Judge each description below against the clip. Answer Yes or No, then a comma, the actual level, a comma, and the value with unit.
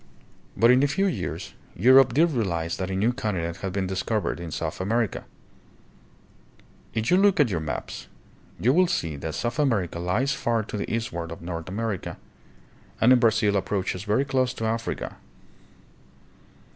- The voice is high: No, low, 110 Hz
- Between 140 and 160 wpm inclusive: No, average, 170 wpm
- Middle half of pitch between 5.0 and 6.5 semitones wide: Yes, wide, 5.6 semitones